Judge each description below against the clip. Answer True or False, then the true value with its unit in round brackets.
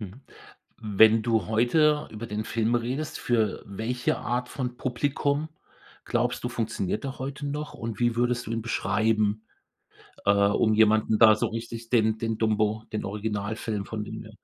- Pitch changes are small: True (2.2 semitones)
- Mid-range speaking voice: False (115 Hz)